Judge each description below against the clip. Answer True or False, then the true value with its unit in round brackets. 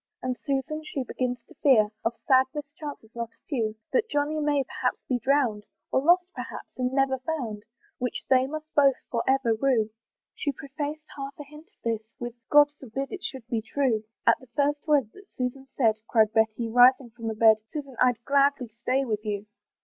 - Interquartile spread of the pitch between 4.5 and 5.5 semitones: False (3.8 semitones)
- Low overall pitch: False (260 Hz)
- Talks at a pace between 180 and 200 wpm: True (195 wpm)